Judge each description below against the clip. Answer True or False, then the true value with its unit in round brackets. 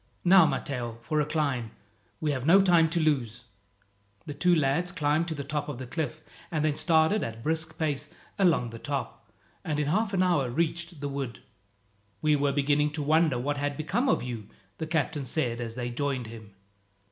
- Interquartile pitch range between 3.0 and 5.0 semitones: True (3.5 semitones)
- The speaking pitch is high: False (150 Hz)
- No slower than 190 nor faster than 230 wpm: True (195 wpm)